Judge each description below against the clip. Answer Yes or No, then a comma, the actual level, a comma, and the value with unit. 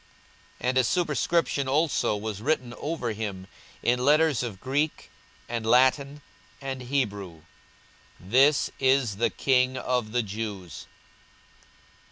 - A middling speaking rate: No, slow, 120 wpm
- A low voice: Yes, low, 125 Hz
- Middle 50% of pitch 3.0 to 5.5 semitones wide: Yes, average, 4.1 semitones